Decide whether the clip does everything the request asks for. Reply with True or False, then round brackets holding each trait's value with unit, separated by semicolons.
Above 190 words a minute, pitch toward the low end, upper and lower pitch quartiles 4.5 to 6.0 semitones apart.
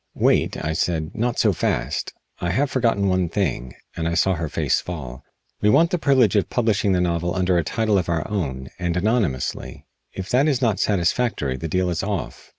True (200 wpm; 90 Hz; 4.9 semitones)